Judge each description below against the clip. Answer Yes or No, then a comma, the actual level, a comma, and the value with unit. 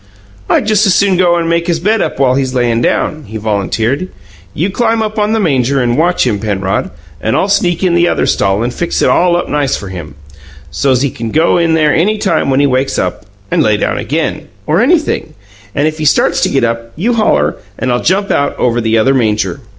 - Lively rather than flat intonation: Yes, wide, 7.2 semitones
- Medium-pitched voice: Yes, medium, 145 Hz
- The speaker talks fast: Yes, fast, 230 wpm